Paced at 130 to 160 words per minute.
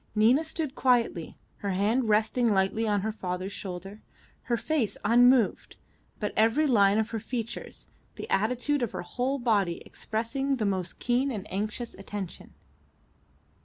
Yes: average, 145 wpm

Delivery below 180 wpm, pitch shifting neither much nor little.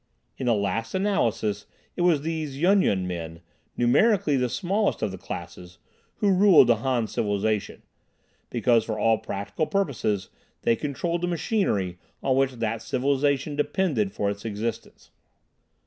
No: average, 145 wpm; wide, 7.5 semitones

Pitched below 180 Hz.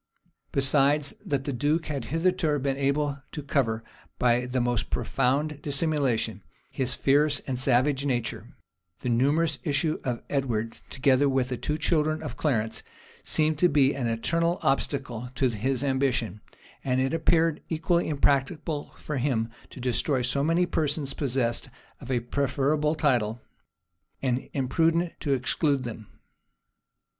Yes: medium, 140 Hz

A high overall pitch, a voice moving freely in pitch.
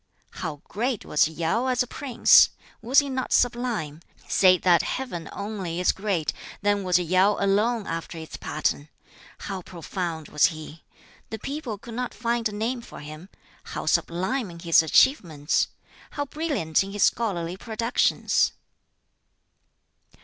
Yes: high, 195 Hz; wide, 6.0 semitones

